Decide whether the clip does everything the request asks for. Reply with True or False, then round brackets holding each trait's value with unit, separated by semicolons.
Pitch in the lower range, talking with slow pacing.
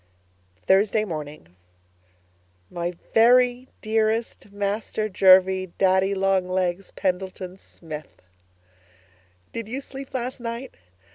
False (195 Hz; 90 wpm)